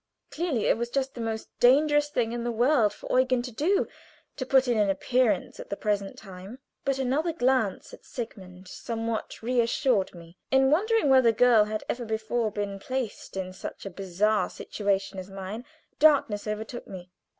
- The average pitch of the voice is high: Yes, high, 230 Hz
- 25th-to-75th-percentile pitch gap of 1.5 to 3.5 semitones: No, average, 4.3 semitones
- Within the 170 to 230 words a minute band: Yes, average, 175 wpm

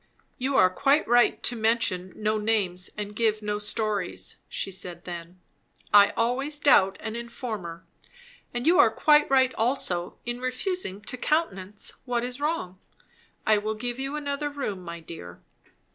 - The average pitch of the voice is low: No, high, 220 Hz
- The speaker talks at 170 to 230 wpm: No, average, 155 wpm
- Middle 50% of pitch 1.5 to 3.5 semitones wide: No, wide, 5.5 semitones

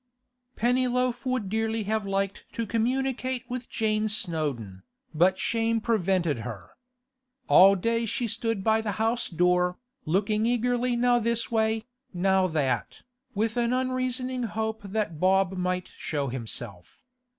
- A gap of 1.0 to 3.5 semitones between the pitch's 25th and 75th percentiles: No, average, 4.5 semitones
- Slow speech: Yes, slow, 130 wpm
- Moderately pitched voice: No, high, 220 Hz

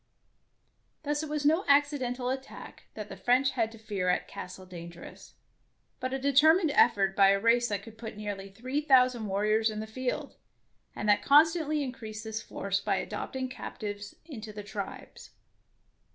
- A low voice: No, high, 230 Hz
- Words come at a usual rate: Yes, average, 165 wpm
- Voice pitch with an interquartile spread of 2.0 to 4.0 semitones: No, average, 4.9 semitones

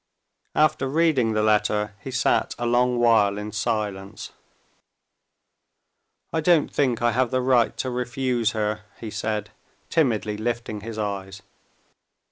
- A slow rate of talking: Yes, slow, 130 wpm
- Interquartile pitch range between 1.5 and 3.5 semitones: Yes, average, 3.1 semitones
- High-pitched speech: No, low, 115 Hz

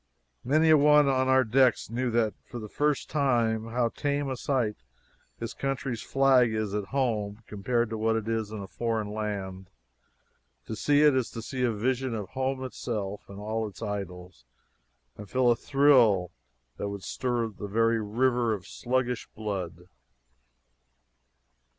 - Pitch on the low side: Yes, low, 115 Hz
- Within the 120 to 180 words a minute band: Yes, average, 160 wpm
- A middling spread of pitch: Yes, average, 3.7 semitones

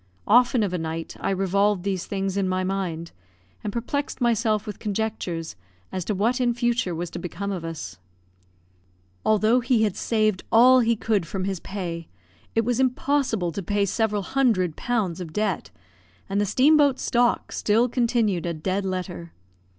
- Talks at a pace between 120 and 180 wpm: Yes, average, 175 wpm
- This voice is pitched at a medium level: No, high, 205 Hz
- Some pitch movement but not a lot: Yes, average, 4.2 semitones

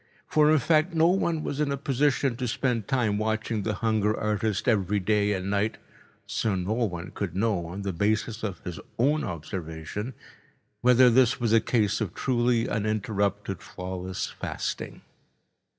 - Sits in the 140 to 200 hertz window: No, low, 110 Hz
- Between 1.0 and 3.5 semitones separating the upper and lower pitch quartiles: No, average, 4.1 semitones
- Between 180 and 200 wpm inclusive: No, average, 160 wpm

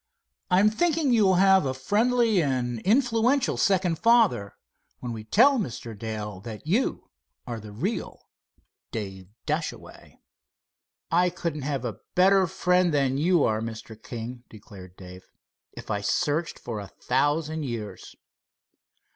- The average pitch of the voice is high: No, medium, 145 Hz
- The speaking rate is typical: No, slow, 130 wpm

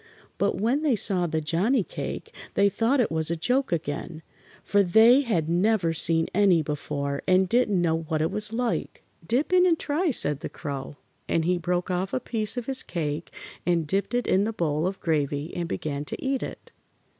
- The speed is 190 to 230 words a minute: Yes, average, 200 wpm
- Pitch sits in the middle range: Yes, medium, 180 Hz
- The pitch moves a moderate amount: No, wide, 5.9 semitones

